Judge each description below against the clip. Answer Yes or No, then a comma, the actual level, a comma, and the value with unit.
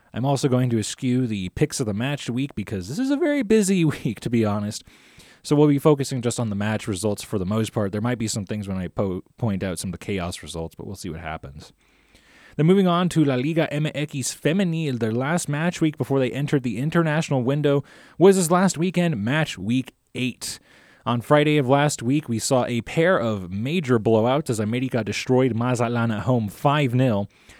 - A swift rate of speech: Yes, fast, 215 wpm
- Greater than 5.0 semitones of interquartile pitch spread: Yes, wide, 5.5 semitones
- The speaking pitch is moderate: No, low, 130 Hz